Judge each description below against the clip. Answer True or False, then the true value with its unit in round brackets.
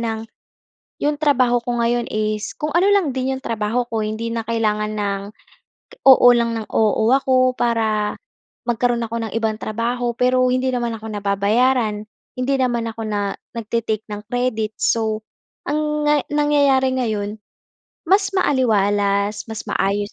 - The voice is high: True (230 Hz)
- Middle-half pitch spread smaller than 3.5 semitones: True (3.1 semitones)